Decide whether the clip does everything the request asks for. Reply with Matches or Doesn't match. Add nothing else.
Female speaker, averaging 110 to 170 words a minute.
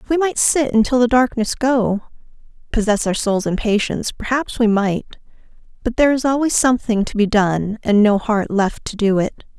Doesn't match